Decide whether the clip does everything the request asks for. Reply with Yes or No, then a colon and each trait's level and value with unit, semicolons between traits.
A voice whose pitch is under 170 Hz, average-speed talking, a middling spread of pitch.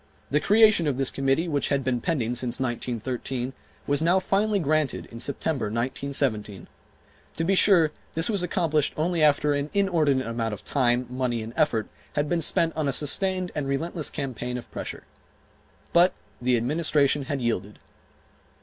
Yes: medium, 140 Hz; average, 160 wpm; average, 4.8 semitones